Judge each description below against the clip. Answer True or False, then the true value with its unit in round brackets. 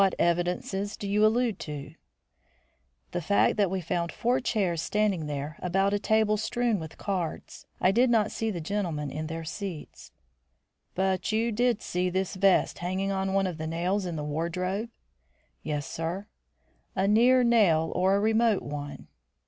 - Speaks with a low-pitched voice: False (190 Hz)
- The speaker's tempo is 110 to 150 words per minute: False (165 wpm)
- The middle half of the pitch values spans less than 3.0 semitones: False (4.1 semitones)